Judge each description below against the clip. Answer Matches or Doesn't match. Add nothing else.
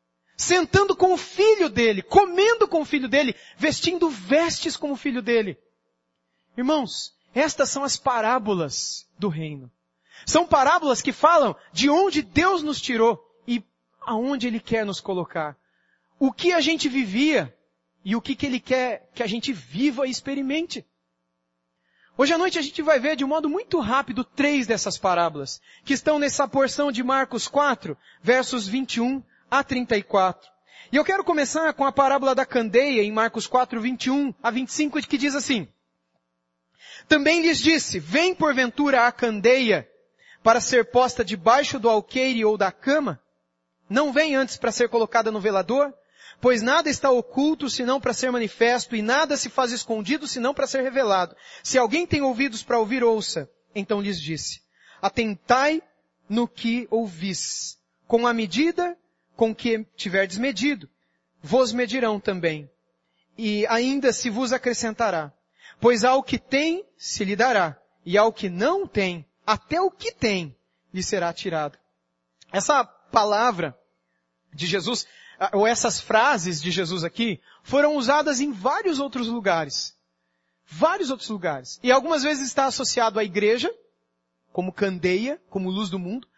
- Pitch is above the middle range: Matches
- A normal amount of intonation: Doesn't match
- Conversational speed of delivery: Matches